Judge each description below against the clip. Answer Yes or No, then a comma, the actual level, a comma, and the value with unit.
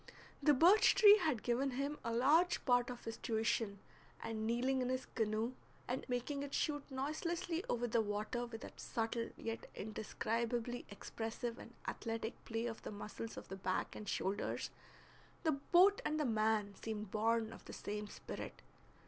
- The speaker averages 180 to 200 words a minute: No, average, 165 wpm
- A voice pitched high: Yes, high, 235 Hz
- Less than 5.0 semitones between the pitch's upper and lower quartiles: Yes, average, 3.6 semitones